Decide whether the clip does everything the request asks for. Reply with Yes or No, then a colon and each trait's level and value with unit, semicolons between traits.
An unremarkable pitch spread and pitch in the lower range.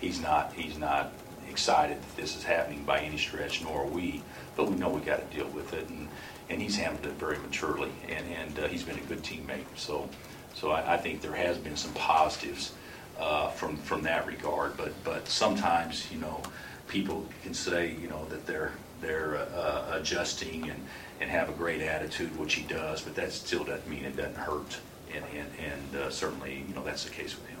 Yes: average, 3.1 semitones; very low, 75 Hz